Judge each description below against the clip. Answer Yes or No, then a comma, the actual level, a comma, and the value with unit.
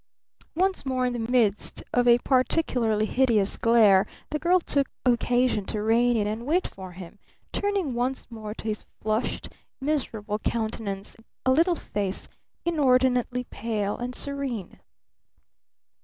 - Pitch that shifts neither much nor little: Yes, average, 3.7 semitones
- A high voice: Yes, high, 240 Hz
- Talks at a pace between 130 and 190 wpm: Yes, slow, 135 wpm